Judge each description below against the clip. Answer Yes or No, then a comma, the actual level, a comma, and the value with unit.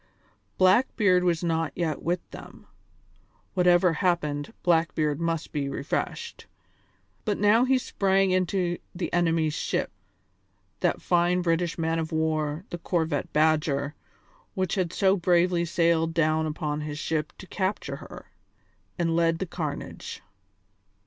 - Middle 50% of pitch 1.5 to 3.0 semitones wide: Yes, narrow, 2.5 semitones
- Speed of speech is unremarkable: No, slow, 130 wpm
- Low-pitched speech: No, medium, 170 Hz